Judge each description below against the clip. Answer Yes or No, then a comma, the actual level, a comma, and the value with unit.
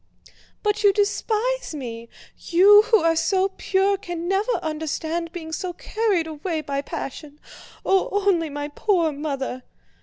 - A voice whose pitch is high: Yes, very high, 340 Hz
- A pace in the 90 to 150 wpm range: Yes, average, 140 wpm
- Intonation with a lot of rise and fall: No, average, 4.6 semitones